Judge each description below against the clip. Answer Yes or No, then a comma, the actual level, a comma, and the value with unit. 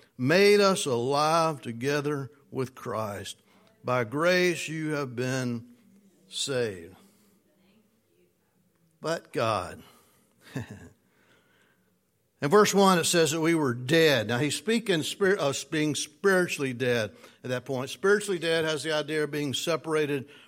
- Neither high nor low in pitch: Yes, medium, 150 Hz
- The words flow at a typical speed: No, slow, 125 wpm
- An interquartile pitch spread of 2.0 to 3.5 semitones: No, average, 4.5 semitones